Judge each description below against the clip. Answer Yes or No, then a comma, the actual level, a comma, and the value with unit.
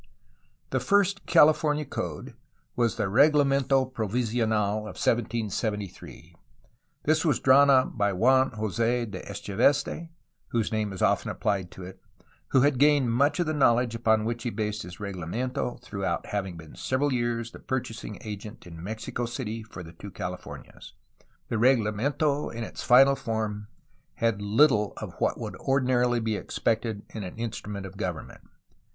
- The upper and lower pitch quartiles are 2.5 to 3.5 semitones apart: No, average, 4.0 semitones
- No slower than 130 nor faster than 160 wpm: Yes, average, 155 wpm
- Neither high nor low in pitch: No, low, 115 Hz